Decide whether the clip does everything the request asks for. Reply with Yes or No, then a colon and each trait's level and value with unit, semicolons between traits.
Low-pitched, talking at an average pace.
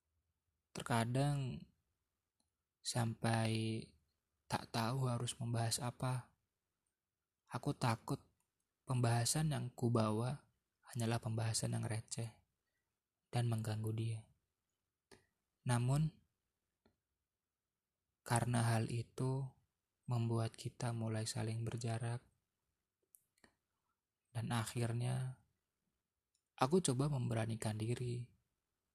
No: low, 115 Hz; slow, 70 wpm